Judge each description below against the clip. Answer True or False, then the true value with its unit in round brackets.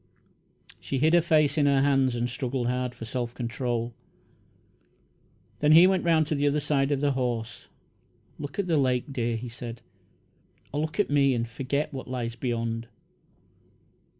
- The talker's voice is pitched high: False (135 Hz)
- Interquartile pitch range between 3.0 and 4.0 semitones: True (3.4 semitones)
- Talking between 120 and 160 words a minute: False (170 wpm)